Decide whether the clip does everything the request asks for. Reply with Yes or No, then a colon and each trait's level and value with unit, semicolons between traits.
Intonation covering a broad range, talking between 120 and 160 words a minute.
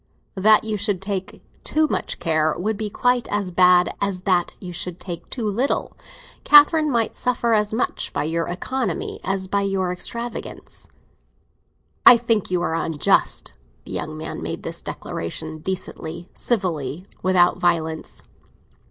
No: average, 4.3 semitones; average, 150 wpm